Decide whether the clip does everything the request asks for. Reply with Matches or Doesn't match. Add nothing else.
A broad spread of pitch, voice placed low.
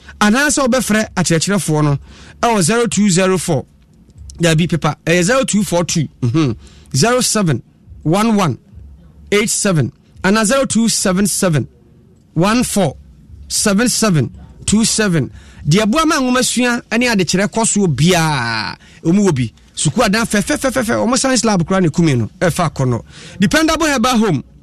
Doesn't match